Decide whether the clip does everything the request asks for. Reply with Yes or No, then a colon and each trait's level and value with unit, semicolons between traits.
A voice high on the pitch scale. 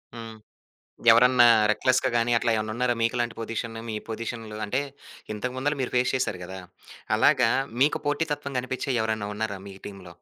No: low, 115 Hz